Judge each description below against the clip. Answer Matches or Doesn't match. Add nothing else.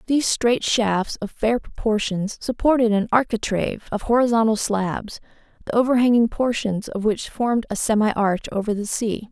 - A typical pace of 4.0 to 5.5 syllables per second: Matches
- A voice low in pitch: Doesn't match